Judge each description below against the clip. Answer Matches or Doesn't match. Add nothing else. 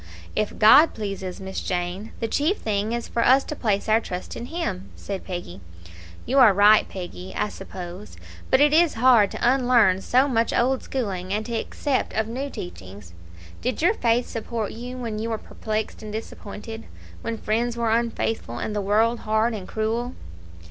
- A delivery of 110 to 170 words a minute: Doesn't match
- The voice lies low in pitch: Doesn't match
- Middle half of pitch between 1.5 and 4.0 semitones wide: Matches